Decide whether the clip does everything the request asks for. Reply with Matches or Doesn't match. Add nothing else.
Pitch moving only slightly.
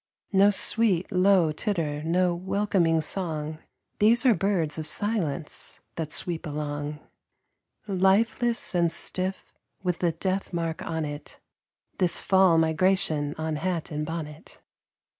Doesn't match